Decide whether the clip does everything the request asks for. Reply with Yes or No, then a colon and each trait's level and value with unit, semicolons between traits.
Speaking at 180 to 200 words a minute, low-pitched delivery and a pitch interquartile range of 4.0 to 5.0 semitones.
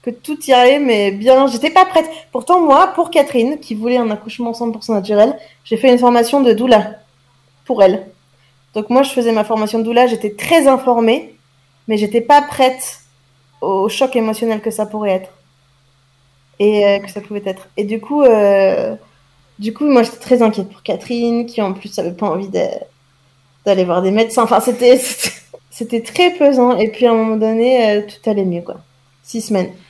No: average, 190 wpm; high, 225 Hz; average, 4.4 semitones